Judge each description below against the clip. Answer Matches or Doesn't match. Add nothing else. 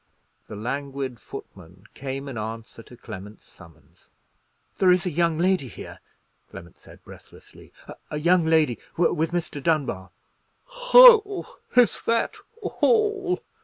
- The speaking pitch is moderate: Matches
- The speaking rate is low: Matches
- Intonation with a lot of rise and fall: Matches